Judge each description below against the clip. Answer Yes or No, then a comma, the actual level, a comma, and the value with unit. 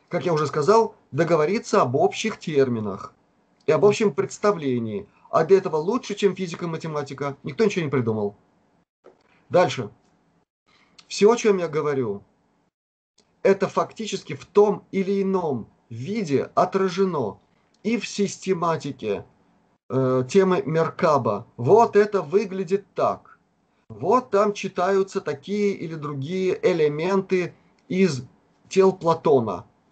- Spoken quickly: No, average, 115 wpm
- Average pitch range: Yes, average, 4.9 semitones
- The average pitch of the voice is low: No, high, 190 Hz